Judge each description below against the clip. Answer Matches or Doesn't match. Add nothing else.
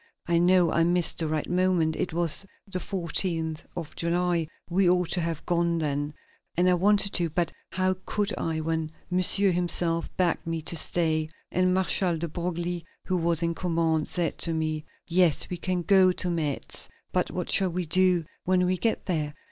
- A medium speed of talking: Matches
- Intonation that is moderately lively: Doesn't match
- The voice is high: Doesn't match